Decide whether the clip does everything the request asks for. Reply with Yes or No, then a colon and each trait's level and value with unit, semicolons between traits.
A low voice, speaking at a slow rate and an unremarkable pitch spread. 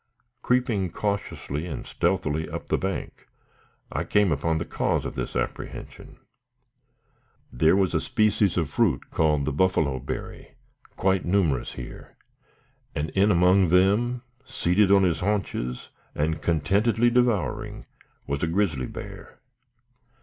Yes: very low, 90 Hz; slow, 130 wpm; average, 4.7 semitones